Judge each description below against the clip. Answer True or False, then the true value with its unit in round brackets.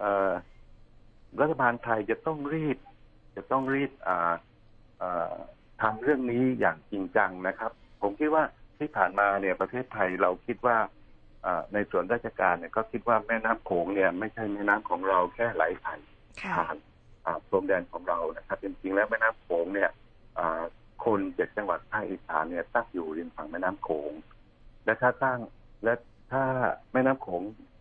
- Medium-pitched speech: False (110 Hz)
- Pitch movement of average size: True (4.4 semitones)